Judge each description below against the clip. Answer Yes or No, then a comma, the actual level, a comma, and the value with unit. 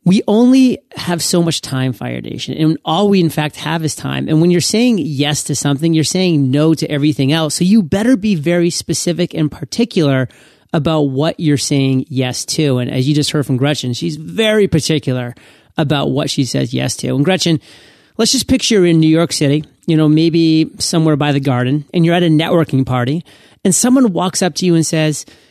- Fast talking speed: Yes, fast, 210 wpm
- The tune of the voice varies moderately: Yes, average, 3.5 semitones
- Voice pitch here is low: No, medium, 155 Hz